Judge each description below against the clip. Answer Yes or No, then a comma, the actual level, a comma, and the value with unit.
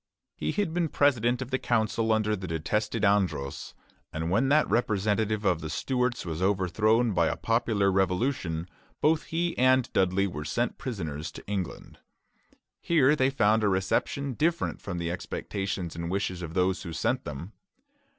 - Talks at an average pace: Yes, average, 160 wpm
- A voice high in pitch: No, low, 105 Hz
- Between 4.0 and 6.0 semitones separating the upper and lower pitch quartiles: Yes, wide, 5.6 semitones